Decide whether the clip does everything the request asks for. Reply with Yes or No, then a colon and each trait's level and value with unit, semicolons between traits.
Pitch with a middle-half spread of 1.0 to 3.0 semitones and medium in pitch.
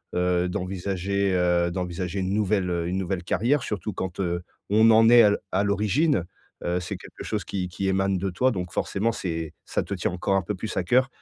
No: narrow, 2.5 semitones; very low, 95 Hz